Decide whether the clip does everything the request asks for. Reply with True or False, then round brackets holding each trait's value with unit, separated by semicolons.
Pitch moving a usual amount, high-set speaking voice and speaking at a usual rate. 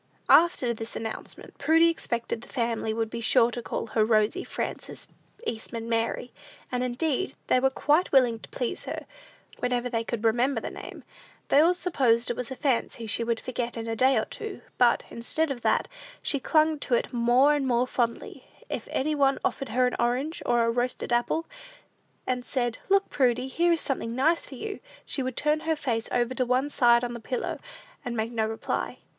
True (3.1 semitones; 245 Hz; 195 wpm)